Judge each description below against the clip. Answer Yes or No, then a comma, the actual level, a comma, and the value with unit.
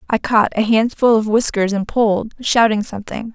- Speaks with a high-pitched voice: Yes, high, 220 Hz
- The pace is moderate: Yes, average, 180 wpm